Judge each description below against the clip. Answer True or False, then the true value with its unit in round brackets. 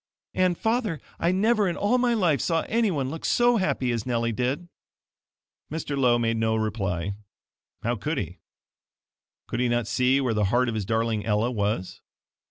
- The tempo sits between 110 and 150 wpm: False (175 wpm)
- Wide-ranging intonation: True (7.8 semitones)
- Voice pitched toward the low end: True (125 Hz)